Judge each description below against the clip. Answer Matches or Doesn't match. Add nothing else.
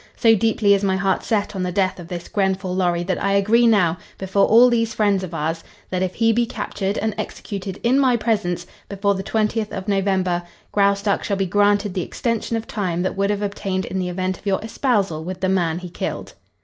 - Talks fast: Matches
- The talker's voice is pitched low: Doesn't match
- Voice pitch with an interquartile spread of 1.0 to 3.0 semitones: Matches